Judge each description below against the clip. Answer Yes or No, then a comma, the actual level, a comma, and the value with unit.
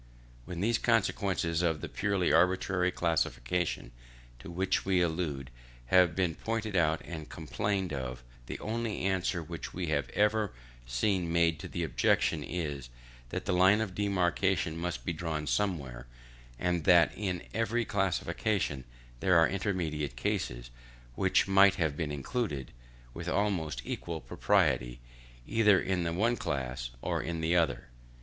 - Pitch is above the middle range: No, very low, 85 Hz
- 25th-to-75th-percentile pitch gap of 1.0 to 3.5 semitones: No, average, 4.1 semitones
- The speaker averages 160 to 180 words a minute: No, average, 145 wpm